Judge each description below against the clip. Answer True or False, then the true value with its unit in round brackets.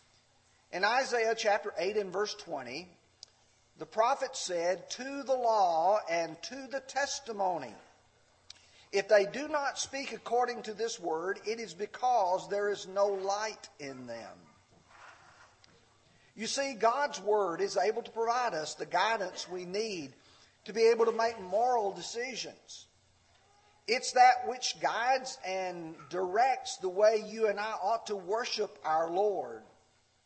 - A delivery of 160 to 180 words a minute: False (140 wpm)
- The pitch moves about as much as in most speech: True (4.9 semitones)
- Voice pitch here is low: False (220 Hz)